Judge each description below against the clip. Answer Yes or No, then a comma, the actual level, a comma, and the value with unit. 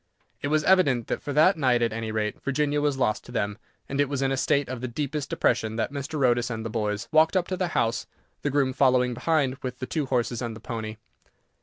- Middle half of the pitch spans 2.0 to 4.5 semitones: Yes, average, 3.7 semitones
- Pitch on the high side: No, low, 130 Hz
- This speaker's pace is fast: Yes, fast, 245 wpm